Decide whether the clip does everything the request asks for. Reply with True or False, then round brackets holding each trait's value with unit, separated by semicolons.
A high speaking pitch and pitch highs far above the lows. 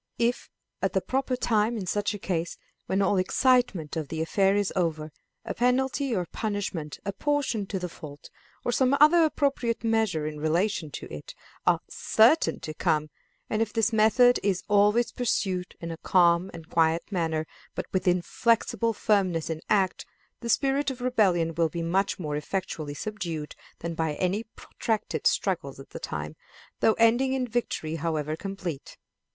True (195 Hz; 5.8 semitones)